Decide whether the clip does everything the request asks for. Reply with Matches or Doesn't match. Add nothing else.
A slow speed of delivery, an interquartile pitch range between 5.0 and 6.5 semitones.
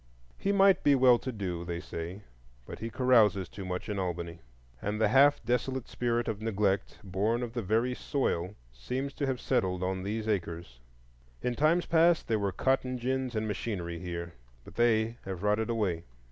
Doesn't match